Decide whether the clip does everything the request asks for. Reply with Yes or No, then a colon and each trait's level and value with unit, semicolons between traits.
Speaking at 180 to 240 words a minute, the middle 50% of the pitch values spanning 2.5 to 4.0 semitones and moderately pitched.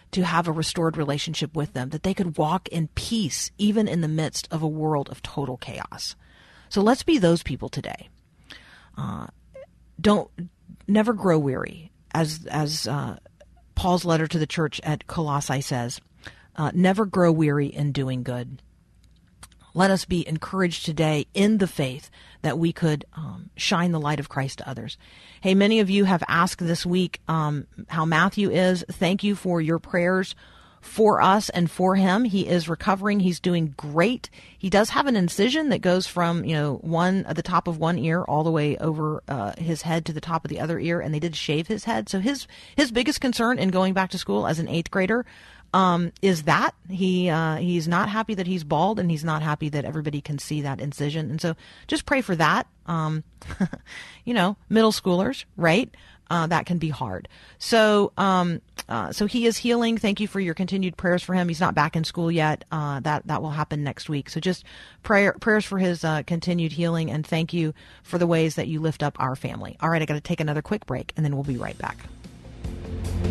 Yes: fast, 205 wpm; average, 3.7 semitones; medium, 165 Hz